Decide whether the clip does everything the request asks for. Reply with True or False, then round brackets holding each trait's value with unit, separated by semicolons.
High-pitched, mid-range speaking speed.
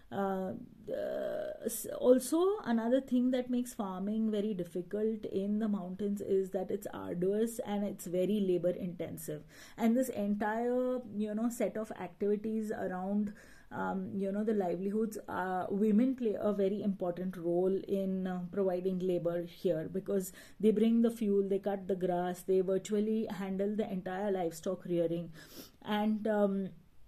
False (200 Hz; 145 wpm)